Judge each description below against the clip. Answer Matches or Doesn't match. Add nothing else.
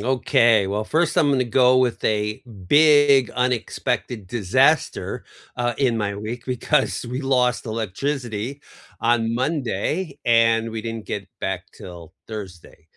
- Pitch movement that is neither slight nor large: Matches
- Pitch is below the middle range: Matches